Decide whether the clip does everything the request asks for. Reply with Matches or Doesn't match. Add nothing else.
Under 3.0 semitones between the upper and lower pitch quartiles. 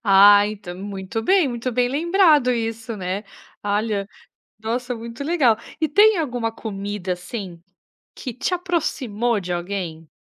Doesn't match